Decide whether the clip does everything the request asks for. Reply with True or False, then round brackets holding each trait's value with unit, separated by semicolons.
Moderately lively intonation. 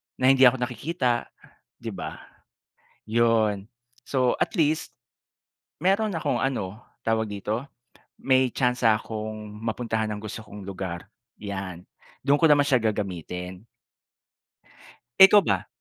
True (4.2 semitones)